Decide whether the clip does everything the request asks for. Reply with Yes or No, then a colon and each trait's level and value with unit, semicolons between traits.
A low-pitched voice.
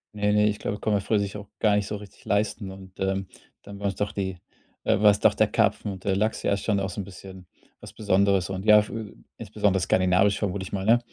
Yes: low, 100 Hz